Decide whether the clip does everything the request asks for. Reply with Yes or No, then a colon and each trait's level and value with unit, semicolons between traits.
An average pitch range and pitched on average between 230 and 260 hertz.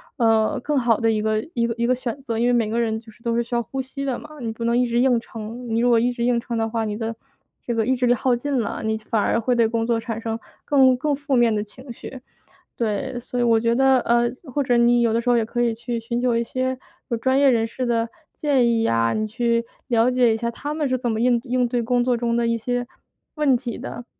No: narrow, 1.7 semitones; high, 235 Hz